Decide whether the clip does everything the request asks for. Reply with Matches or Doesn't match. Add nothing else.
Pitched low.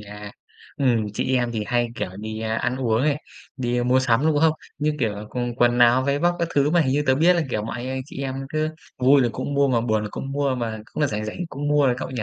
Matches